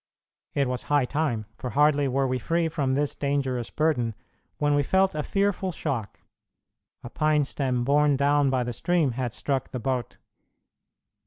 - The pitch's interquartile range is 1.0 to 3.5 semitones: Yes, average, 2.9 semitones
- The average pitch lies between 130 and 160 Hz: Yes, medium, 140 Hz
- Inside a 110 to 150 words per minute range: No, average, 165 wpm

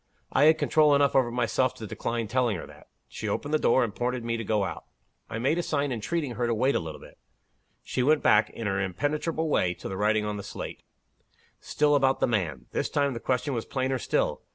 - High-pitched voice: No, low, 125 Hz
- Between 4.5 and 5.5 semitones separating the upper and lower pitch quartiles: Yes, average, 5.0 semitones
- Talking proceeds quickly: Yes, fast, 230 wpm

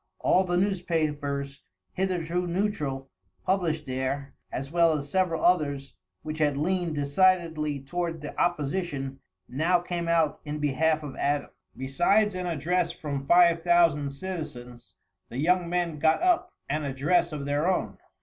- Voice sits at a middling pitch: Yes, medium, 160 Hz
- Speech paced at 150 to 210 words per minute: No, average, 140 wpm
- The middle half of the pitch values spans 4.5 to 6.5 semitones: No, average, 3.9 semitones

